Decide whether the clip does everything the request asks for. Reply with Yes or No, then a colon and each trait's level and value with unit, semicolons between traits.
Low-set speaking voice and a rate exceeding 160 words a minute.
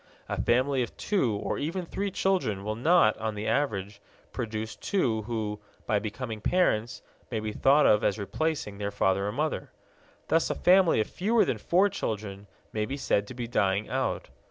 Yes: low, 115 Hz; average, 180 wpm